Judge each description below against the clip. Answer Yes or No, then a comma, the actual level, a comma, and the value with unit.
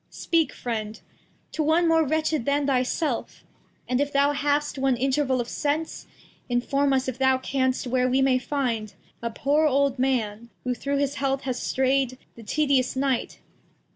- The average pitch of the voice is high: Yes, very high, 270 Hz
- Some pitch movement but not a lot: No, narrow, 2.2 semitones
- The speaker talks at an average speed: Yes, average, 170 wpm